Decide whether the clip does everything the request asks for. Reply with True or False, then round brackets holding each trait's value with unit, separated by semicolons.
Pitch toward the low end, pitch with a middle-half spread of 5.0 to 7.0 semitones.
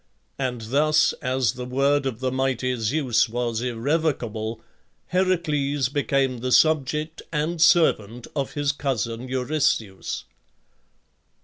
False (130 Hz; 3.5 semitones)